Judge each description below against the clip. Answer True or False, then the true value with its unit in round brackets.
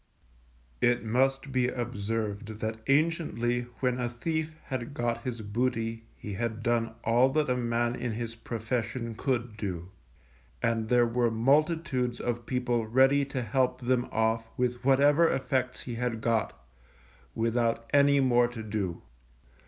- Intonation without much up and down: True (2.2 semitones)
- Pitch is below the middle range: True (120 Hz)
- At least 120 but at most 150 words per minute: True (145 wpm)